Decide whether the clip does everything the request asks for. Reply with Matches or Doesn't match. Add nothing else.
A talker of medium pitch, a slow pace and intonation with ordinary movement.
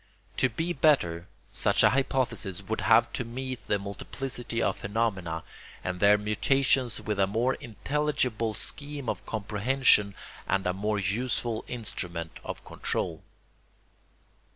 Doesn't match